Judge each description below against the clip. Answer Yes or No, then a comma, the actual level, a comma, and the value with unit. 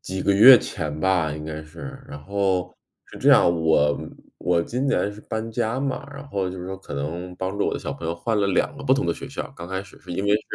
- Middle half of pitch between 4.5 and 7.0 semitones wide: Yes, average, 4.9 semitones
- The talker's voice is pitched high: No, very low, 95 Hz